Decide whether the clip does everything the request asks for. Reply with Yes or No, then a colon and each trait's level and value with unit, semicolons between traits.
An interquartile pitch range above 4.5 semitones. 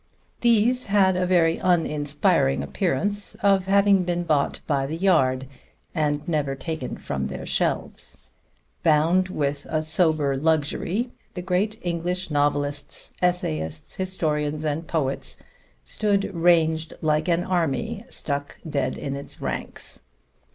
No: average, 4.1 semitones